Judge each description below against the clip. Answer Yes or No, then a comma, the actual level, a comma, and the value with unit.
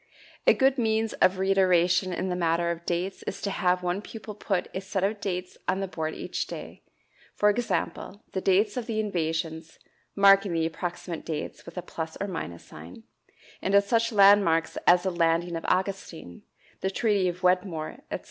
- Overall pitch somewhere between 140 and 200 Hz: Yes, medium, 185 Hz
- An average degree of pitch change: Yes, average, 3.0 semitones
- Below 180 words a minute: No, average, 185 wpm